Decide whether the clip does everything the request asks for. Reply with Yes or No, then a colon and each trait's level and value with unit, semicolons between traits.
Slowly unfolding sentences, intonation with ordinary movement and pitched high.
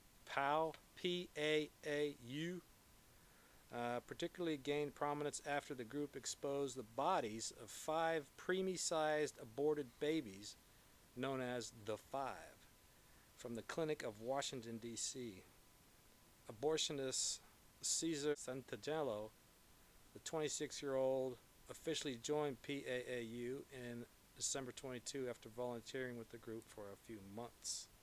No: slow, 100 wpm; average, 4.0 semitones; low, 135 Hz